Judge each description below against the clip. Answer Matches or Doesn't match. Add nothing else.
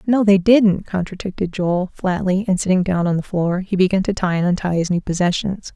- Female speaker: Matches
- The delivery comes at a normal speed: Doesn't match